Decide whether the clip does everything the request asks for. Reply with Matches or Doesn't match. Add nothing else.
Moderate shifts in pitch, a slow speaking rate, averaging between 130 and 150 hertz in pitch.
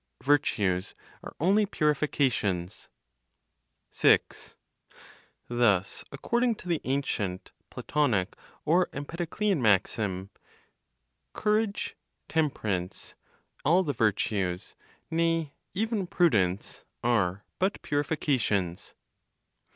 Doesn't match